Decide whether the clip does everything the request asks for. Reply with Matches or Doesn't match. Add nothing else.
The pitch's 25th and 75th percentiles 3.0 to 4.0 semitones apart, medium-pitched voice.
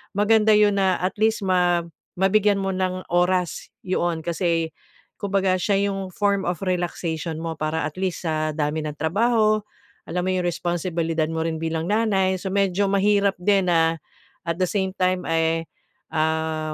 Matches